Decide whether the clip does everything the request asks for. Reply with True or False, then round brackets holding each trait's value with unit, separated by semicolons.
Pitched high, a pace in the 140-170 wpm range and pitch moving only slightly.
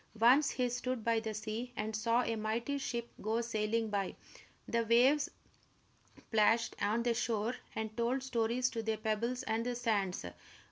True (230 Hz; 160 wpm; 1.9 semitones)